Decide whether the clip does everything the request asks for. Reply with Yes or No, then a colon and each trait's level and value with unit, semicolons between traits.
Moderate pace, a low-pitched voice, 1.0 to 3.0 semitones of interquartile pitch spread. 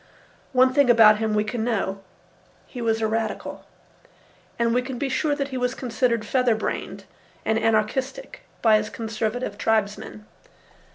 No: average, 155 wpm; high, 225 Hz; narrow, 2.6 semitones